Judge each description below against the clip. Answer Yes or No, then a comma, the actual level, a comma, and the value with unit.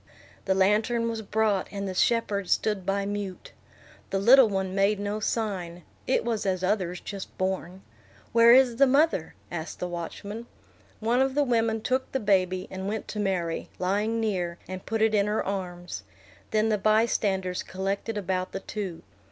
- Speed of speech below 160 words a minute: No, average, 170 wpm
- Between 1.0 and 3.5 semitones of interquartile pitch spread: Yes, average, 3.0 semitones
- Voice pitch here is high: Yes, high, 200 Hz